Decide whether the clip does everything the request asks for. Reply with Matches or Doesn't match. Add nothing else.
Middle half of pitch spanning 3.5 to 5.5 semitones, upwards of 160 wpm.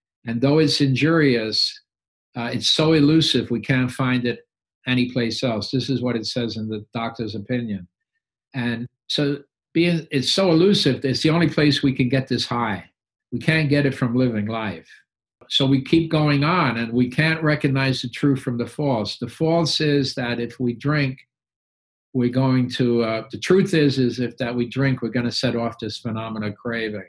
Matches